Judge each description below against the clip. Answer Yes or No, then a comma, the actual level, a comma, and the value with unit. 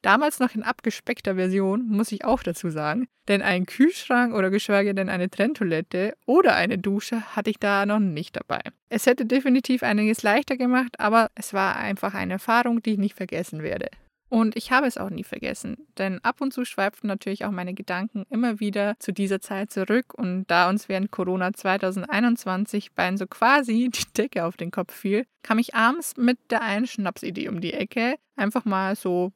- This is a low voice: No, high, 210 Hz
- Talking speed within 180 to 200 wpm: Yes, fast, 190 wpm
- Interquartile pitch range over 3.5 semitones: Yes, average, 3.9 semitones